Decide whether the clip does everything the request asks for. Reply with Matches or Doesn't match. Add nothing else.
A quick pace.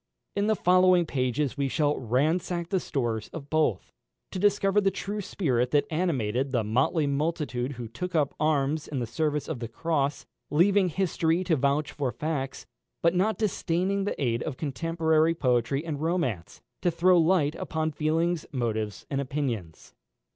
Doesn't match